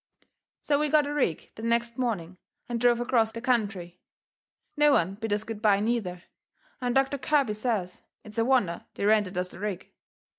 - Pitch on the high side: Yes, high, 225 Hz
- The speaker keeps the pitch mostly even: No, average, 3.8 semitones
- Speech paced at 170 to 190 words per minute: Yes, average, 185 wpm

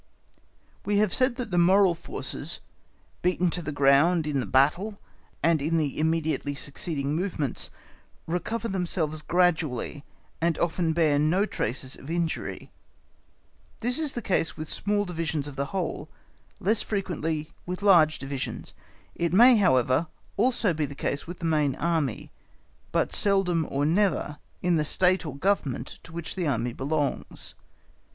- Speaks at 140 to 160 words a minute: Yes, average, 150 wpm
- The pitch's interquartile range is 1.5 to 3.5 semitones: No, average, 4.1 semitones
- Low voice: No, medium, 165 Hz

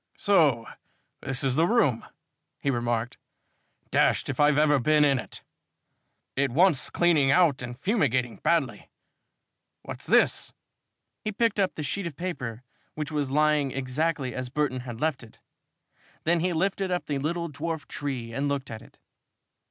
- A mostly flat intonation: No, average, 4.5 semitones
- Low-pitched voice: No, medium, 145 Hz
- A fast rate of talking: No, average, 155 wpm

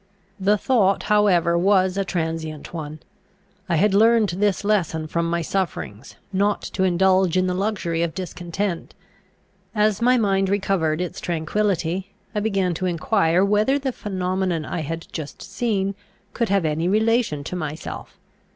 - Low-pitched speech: No, high, 190 Hz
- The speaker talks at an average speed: Yes, average, 150 wpm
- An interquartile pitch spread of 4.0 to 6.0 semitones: No, average, 3.5 semitones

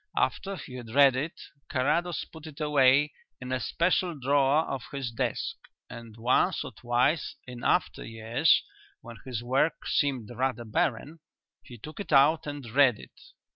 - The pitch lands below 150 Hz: Yes, low, 135 Hz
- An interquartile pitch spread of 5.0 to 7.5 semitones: No, average, 3.8 semitones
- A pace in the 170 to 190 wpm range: No, average, 160 wpm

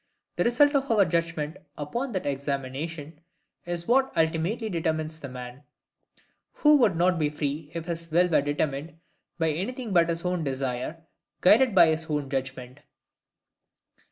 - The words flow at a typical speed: Yes, average, 150 wpm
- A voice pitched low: No, medium, 165 Hz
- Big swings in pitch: No, average, 3.7 semitones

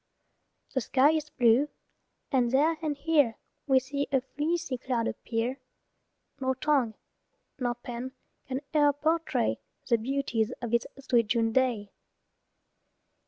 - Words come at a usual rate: No, slow, 125 wpm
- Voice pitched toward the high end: Yes, very high, 260 Hz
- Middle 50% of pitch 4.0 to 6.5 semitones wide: No, average, 3.4 semitones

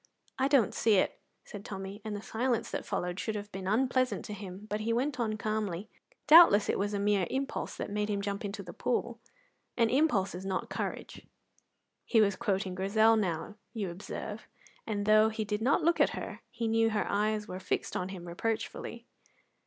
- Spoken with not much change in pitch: Yes, narrow, 2.3 semitones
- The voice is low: No, high, 210 Hz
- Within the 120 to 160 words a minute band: No, average, 195 wpm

